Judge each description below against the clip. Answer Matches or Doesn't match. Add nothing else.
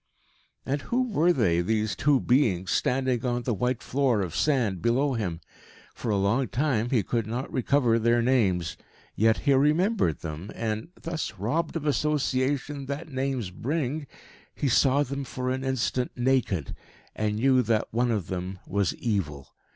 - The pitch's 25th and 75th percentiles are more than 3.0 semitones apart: Matches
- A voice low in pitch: Matches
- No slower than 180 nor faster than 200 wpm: Doesn't match